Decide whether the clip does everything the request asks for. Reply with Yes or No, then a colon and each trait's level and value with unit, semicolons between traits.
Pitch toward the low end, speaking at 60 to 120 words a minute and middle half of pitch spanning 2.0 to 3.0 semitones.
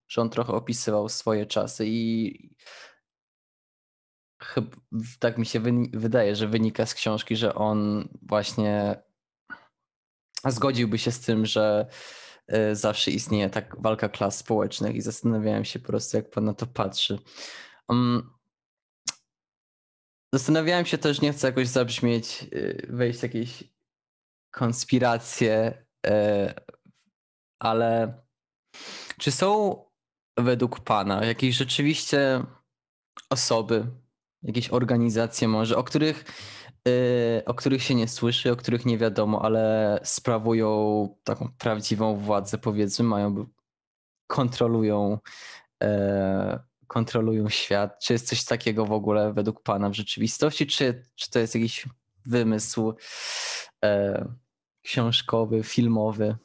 Yes: low, 115 Hz; average, 115 wpm; narrow, 2.4 semitones